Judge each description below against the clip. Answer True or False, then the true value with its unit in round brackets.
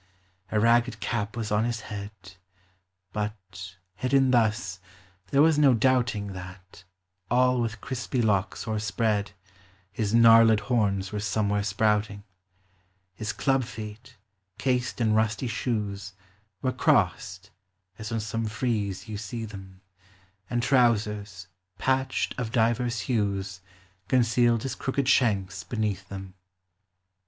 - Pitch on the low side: True (110 Hz)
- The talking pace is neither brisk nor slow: False (125 wpm)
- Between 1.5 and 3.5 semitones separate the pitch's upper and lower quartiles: True (2.9 semitones)